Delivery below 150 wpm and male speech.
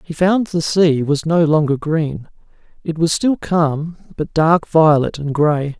No: average, 175 wpm; male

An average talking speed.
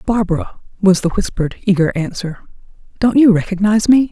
Yes: average, 145 wpm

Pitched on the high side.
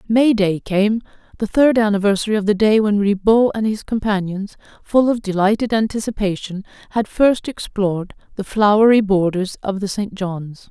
Yes: high, 205 Hz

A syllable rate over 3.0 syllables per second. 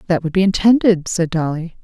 Yes: 5.6 syllables/s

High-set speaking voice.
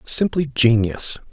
No: low, 130 Hz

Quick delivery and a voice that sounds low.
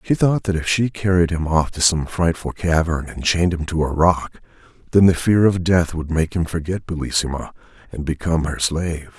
Yes: fast, 210 wpm; very low, 85 Hz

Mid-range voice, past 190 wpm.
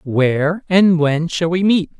No: medium, 170 Hz; average, 180 wpm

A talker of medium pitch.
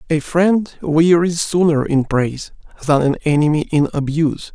Yes: medium, 155 Hz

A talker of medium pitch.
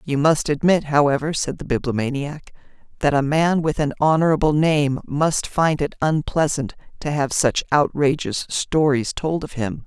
Yes: medium, 145 Hz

